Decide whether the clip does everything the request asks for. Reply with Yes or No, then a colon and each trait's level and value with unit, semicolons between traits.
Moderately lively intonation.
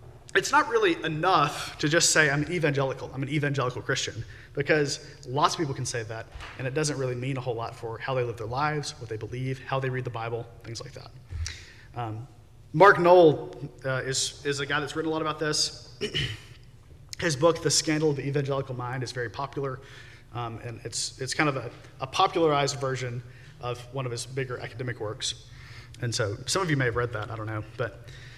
Yes: average, 3.4 semitones